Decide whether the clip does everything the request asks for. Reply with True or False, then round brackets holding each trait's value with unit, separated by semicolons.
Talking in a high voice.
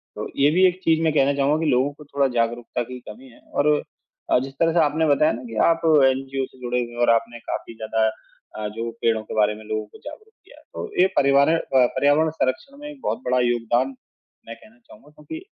False (135 Hz)